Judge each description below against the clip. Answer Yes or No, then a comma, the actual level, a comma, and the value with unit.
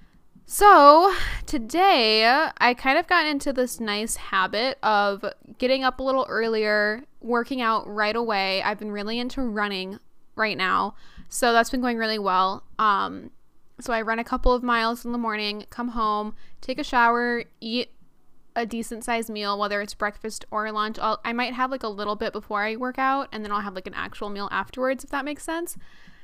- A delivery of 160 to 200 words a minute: Yes, average, 190 wpm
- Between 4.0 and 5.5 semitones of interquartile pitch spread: No, average, 3.4 semitones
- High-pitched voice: Yes, high, 230 Hz